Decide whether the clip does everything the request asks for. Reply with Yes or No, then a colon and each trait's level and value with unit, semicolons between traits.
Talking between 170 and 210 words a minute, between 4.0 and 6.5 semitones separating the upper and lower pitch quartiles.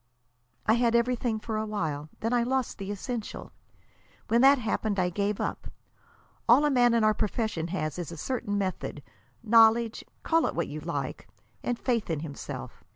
No: average, 175 wpm; average, 3.6 semitones